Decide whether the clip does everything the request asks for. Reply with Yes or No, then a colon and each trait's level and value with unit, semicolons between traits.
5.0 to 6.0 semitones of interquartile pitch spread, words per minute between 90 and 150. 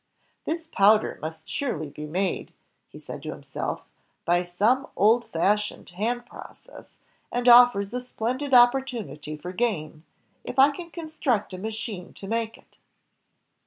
Yes: wide, 5.5 semitones; average, 145 wpm